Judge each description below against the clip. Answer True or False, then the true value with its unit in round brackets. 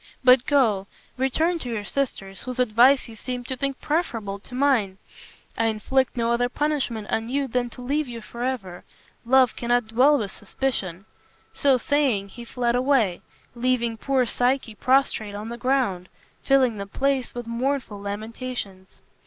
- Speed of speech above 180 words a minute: False (155 wpm)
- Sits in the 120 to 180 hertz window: False (245 Hz)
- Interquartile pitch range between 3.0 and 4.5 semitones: True (3.4 semitones)